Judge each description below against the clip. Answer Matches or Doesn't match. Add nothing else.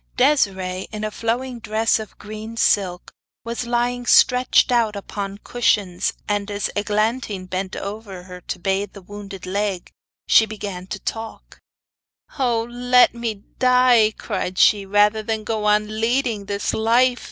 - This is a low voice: Doesn't match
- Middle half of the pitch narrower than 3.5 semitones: Matches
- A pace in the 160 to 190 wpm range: Doesn't match